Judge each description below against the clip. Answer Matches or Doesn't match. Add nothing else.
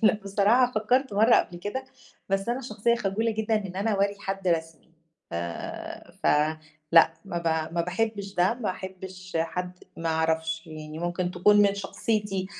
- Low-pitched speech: Doesn't match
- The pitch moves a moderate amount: Matches